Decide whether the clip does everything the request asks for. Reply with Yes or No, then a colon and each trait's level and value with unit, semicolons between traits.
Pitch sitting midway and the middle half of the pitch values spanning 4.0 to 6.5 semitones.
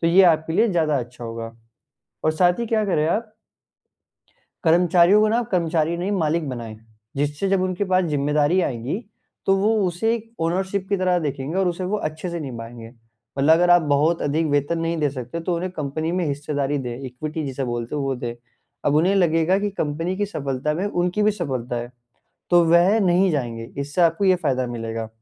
Yes: medium, 165 Hz; average, 4.7 semitones